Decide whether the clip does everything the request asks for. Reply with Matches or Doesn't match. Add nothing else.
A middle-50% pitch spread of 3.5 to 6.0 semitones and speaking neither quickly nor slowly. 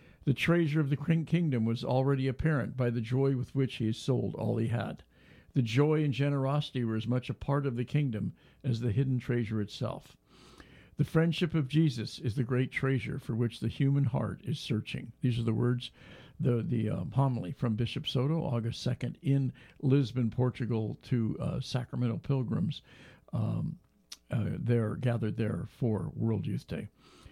Doesn't match